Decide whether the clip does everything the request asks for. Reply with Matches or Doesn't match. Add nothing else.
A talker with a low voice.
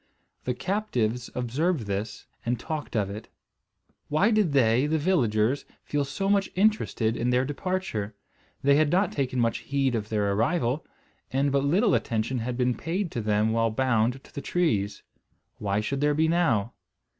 Matches